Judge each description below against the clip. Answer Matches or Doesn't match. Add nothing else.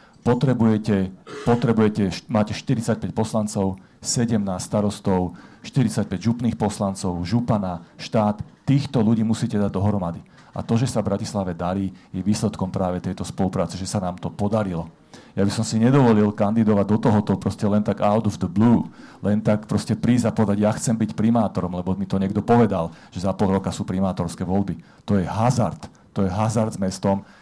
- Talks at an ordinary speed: Doesn't match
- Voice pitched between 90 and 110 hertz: Matches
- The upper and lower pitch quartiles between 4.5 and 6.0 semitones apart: Doesn't match